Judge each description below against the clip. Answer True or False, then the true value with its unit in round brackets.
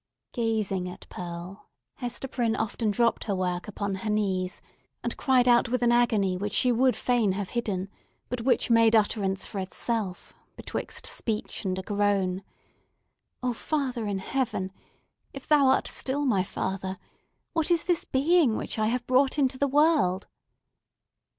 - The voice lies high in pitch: True (225 Hz)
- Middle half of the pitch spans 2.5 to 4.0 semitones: False (4.8 semitones)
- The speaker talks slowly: False (150 wpm)